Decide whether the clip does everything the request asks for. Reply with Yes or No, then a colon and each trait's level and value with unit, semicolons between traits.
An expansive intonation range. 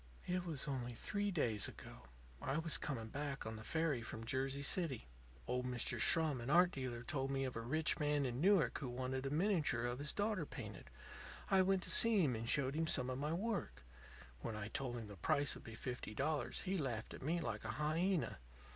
No: average, 5.0 semitones